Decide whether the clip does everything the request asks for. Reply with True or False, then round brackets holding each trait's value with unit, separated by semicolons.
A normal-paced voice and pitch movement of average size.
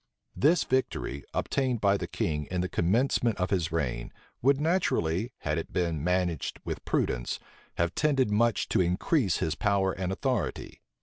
False (160 wpm; 6.9 semitones)